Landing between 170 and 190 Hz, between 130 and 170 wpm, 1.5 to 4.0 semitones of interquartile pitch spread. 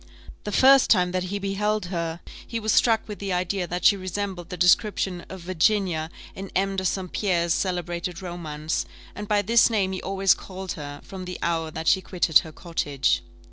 No: medium, 185 Hz; average, 190 wpm; narrow, 2.5 semitones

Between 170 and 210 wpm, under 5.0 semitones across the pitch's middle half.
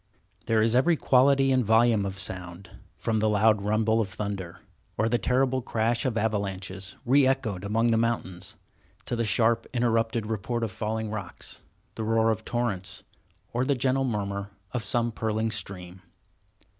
No: average, 160 wpm; average, 2.9 semitones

